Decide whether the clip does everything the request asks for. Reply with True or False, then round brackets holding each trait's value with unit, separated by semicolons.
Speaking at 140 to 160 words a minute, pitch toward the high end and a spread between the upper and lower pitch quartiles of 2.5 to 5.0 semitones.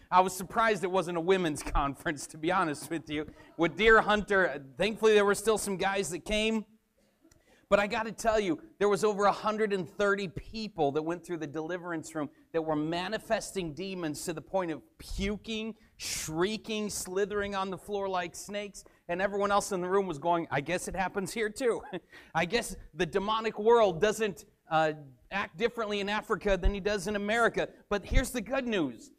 False (190 wpm; 200 Hz; 3.7 semitones)